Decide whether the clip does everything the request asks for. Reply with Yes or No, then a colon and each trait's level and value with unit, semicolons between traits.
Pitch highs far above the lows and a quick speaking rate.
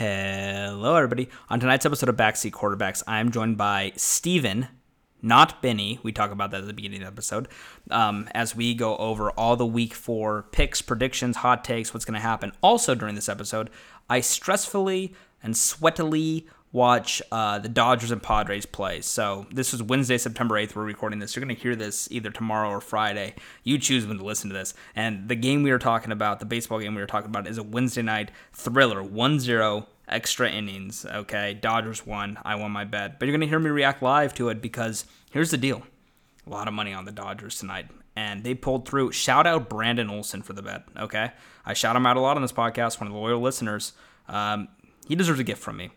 No: average, 3.2 semitones; fast, 215 wpm